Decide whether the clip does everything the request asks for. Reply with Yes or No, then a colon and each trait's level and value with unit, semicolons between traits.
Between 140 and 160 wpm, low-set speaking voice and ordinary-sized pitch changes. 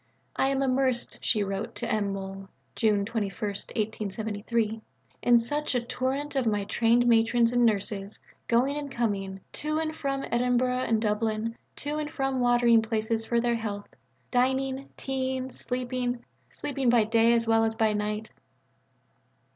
No: average, 155 wpm; high, 235 Hz; average, 3.0 semitones